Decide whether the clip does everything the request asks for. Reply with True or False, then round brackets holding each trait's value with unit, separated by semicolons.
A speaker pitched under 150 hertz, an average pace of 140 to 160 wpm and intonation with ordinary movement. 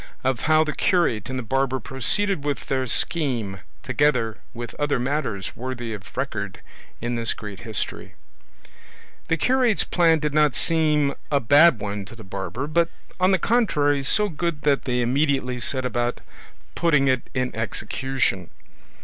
True (135 Hz; 155 wpm; 4.5 semitones)